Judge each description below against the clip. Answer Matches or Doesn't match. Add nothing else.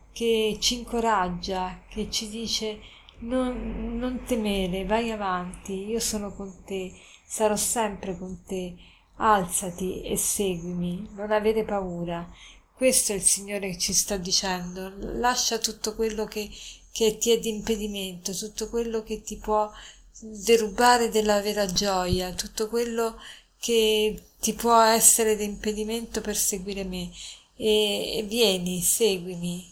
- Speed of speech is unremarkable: Matches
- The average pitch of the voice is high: Matches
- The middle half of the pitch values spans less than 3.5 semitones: Matches